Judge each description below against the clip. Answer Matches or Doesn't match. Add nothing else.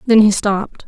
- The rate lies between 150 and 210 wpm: Matches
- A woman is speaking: Matches